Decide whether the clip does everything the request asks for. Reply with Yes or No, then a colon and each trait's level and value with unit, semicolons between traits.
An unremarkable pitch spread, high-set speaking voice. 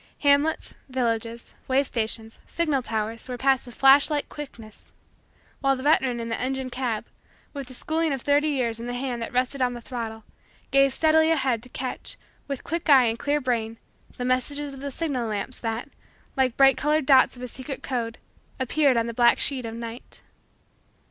Yes: average, 3.1 semitones; very high, 255 Hz